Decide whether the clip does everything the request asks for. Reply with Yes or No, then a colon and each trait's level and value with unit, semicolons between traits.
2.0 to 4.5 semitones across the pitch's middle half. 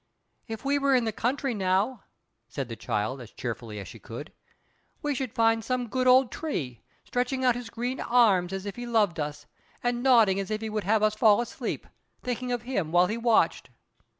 No: average, 4.9 semitones